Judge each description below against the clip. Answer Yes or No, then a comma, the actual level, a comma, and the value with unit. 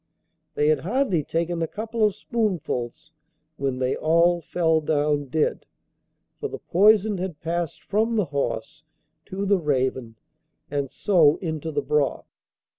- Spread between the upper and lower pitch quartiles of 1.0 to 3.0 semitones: No, average, 5.0 semitones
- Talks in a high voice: No, medium, 165 Hz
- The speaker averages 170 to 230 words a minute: No, average, 140 wpm